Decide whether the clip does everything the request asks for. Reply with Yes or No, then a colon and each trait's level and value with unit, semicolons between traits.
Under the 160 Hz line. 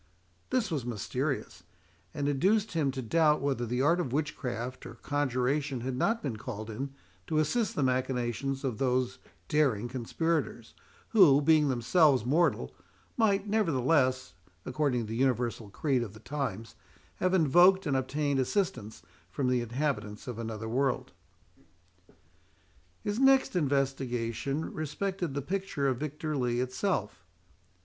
Yes: low, 135 Hz